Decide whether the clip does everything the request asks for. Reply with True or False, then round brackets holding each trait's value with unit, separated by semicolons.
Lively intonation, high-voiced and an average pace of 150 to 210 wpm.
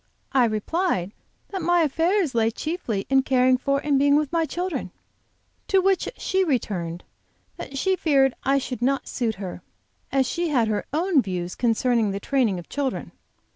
True (6.3 semitones; 270 Hz; 170 wpm)